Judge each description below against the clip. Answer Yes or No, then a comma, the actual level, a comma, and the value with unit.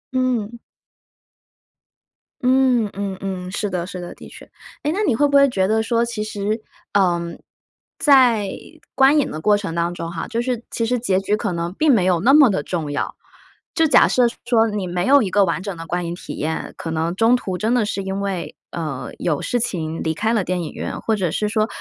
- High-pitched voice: Yes, high, 205 Hz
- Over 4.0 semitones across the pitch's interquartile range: Yes, average, 5.1 semitones